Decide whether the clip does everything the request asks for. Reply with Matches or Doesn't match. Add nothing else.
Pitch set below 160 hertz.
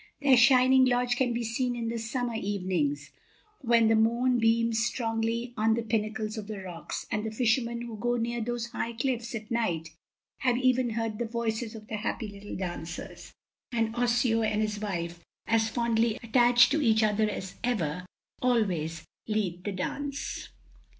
Doesn't match